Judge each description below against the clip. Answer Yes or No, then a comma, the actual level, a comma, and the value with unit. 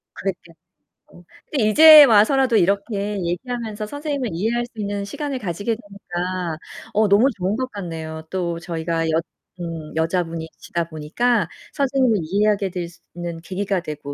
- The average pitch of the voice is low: No, high, 195 Hz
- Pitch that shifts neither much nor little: Yes, average, 5.0 semitones